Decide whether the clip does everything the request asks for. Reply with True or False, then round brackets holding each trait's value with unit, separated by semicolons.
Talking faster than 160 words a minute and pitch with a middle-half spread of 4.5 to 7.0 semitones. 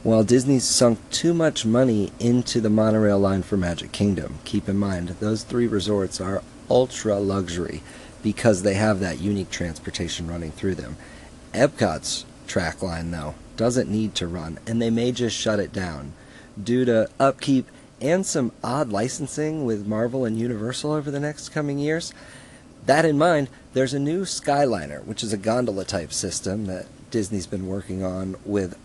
True (170 wpm; 5.0 semitones)